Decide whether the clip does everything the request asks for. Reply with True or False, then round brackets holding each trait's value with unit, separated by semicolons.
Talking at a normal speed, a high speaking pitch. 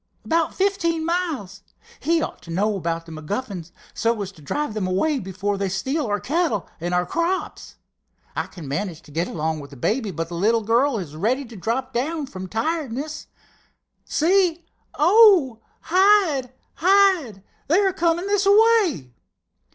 True (160 wpm; 250 Hz)